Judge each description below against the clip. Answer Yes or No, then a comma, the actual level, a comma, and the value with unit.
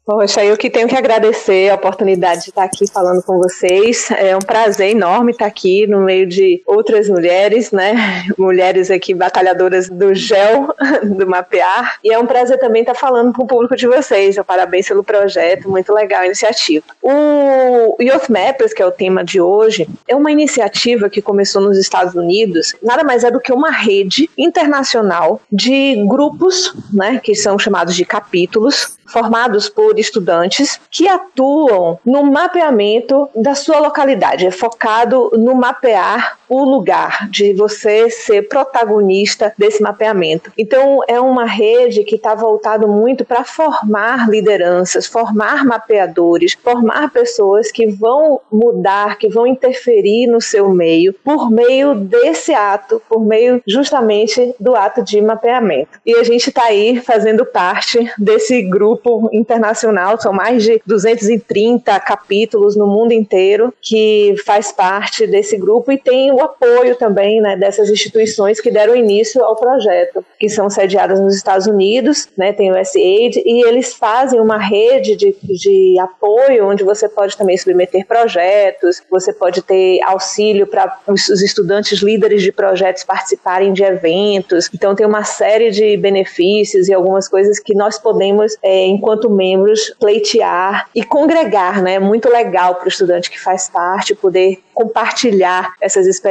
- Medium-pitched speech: No, high, 215 Hz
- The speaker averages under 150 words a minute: No, average, 155 wpm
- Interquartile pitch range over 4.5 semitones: No, average, 3.8 semitones